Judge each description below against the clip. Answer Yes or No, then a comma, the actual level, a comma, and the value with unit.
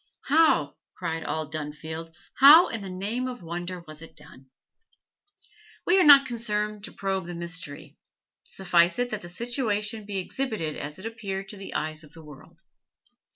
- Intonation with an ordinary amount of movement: No, wide, 5.7 semitones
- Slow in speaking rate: No, average, 165 wpm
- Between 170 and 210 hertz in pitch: Yes, high, 190 Hz